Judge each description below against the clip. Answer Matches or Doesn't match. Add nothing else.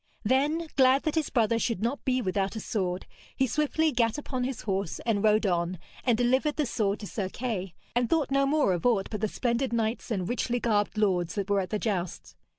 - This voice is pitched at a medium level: Doesn't match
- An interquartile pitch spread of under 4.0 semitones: Doesn't match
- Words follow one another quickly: Matches